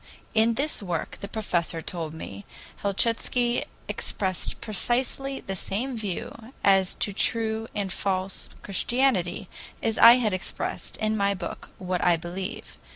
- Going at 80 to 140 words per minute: Yes, slow, 135 wpm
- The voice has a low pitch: No, high, 200 Hz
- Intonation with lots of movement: No, average, 3.8 semitones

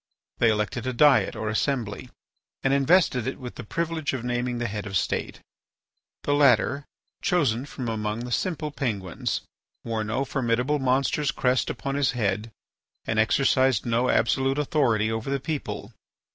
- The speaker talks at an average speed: Yes, average, 160 wpm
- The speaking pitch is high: No, low, 125 Hz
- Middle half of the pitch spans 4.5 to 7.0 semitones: No, average, 3.7 semitones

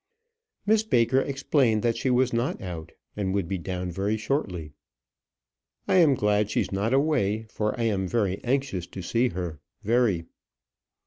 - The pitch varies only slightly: No, average, 5.2 semitones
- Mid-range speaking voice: No, low, 110 Hz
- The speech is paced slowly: No, average, 150 wpm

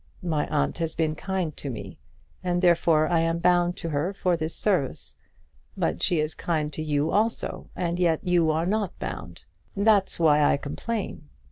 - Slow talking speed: No, average, 175 wpm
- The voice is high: No, medium, 165 Hz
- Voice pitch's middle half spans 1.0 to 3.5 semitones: Yes, average, 2.8 semitones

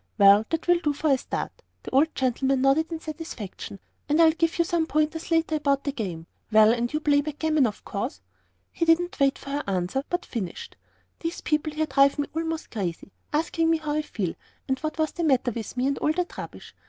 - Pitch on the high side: Yes, very high, 295 Hz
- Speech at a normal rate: No, fast, 225 wpm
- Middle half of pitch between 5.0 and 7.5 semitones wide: No, average, 4.4 semitones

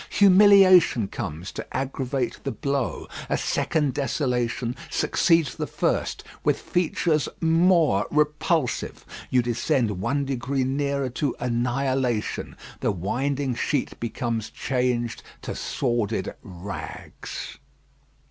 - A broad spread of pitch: No, average, 3.7 semitones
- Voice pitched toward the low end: Yes, low, 130 Hz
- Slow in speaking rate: Yes, slow, 100 wpm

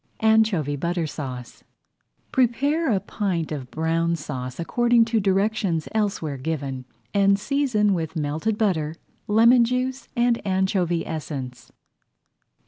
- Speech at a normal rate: No, slow, 125 wpm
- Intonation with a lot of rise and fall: Yes, wide, 6.1 semitones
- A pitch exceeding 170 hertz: Yes, high, 190 Hz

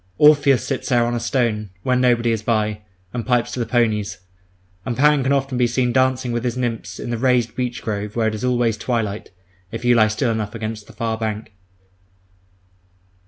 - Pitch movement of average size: No, narrow, 2.3 semitones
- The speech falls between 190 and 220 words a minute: Yes, average, 200 wpm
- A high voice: No, low, 120 Hz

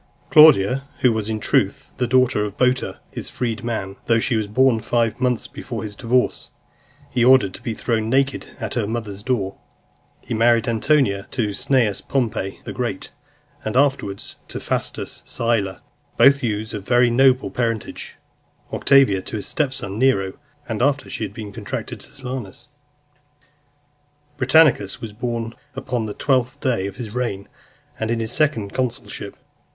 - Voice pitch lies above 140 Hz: No, low, 115 Hz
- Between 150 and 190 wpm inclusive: Yes, average, 155 wpm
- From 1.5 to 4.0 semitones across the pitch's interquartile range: Yes, average, 3.4 semitones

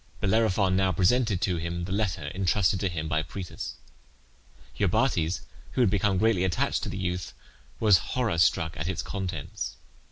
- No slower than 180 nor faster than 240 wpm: No, average, 160 wpm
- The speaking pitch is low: Yes, very low, 95 Hz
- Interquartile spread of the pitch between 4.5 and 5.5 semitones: No, average, 2.9 semitones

